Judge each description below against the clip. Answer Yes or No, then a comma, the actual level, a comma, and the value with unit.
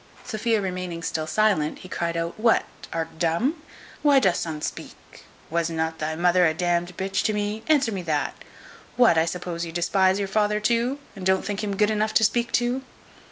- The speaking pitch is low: No, high, 190 Hz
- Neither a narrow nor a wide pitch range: Yes, average, 4.4 semitones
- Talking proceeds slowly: No, average, 200 wpm